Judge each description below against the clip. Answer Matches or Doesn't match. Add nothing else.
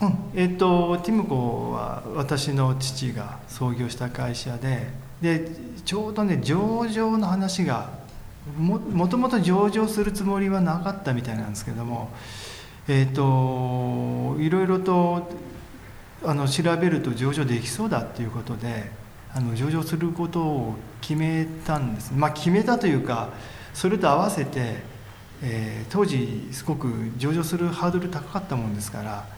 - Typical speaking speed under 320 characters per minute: Matches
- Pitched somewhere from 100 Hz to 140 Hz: Matches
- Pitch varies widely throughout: Matches